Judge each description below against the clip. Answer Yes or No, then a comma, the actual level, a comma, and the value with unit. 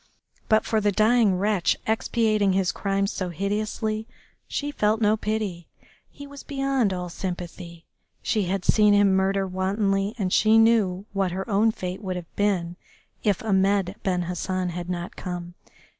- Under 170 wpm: Yes, average, 160 wpm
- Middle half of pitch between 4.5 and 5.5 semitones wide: No, average, 2.8 semitones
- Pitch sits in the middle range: No, high, 195 Hz